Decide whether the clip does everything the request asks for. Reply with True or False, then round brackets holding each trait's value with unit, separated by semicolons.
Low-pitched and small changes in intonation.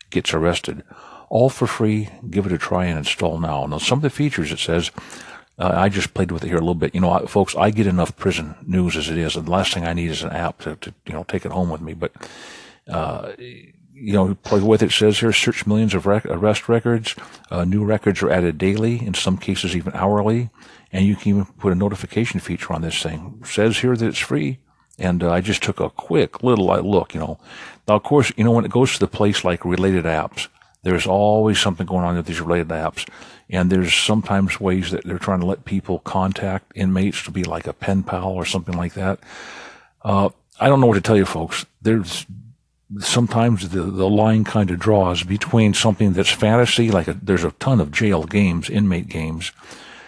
False (95 Hz; 3.6 semitones)